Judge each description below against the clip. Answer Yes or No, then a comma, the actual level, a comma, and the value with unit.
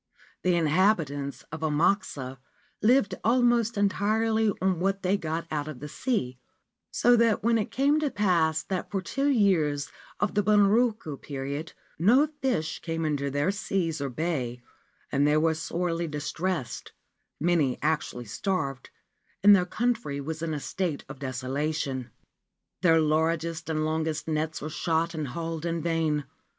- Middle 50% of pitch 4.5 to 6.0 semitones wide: Yes, average, 5.0 semitones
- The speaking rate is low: No, average, 150 wpm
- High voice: No, medium, 165 Hz